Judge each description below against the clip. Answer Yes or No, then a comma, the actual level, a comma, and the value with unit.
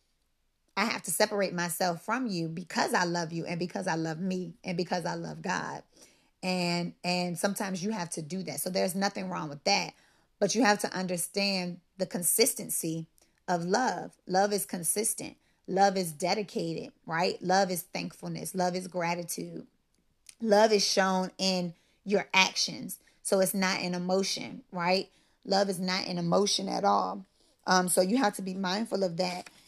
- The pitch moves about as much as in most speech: No, narrow, 2.1 semitones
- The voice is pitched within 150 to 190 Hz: Yes, medium, 185 Hz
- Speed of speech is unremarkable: Yes, average, 170 wpm